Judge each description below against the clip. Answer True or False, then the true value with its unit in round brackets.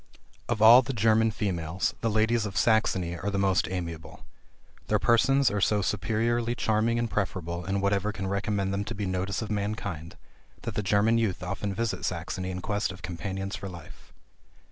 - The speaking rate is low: False (180 wpm)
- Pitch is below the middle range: True (100 Hz)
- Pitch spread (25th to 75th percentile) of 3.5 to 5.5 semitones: False (3.0 semitones)